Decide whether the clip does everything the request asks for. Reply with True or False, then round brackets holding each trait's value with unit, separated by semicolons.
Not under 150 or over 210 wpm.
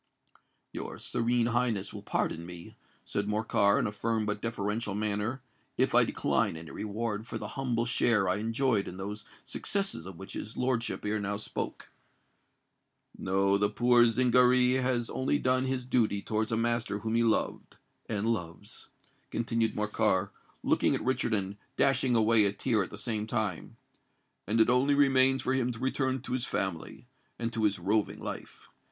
True (165 wpm)